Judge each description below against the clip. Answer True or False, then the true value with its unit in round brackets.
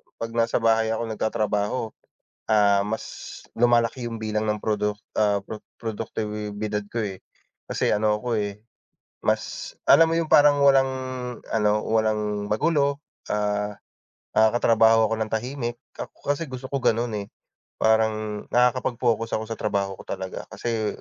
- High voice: False (110 Hz)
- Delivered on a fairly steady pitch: True (2.2 semitones)